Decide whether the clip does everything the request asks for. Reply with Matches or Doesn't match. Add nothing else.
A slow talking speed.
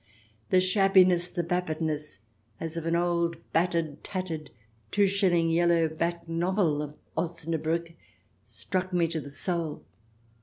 Matches